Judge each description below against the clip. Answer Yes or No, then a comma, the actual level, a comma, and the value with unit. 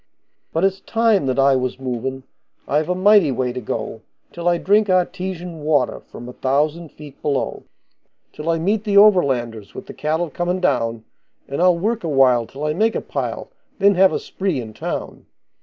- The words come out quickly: No, average, 190 wpm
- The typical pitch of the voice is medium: Yes, medium, 155 Hz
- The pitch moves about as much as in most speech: No, wide, 6.0 semitones